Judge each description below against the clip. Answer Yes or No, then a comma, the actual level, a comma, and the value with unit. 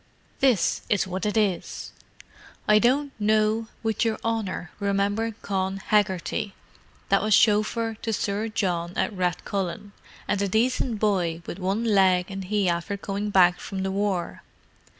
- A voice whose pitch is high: Yes, high, 200 Hz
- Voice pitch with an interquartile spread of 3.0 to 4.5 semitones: No, narrow, 2.4 semitones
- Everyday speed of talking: Yes, average, 150 wpm